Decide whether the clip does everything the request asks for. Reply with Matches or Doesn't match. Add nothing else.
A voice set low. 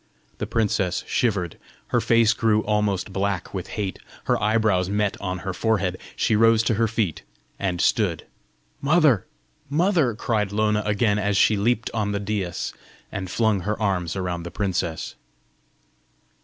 Matches